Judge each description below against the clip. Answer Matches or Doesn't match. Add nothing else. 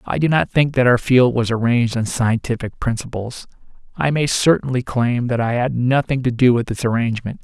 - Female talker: Doesn't match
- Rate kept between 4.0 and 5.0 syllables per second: Doesn't match